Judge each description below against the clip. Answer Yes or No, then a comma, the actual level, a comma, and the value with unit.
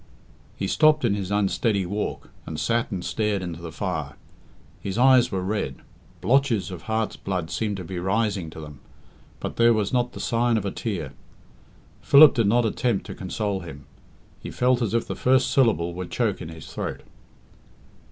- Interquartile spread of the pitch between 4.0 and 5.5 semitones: Yes, average, 4.3 semitones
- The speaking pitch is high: No, low, 105 Hz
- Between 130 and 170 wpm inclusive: No, average, 180 wpm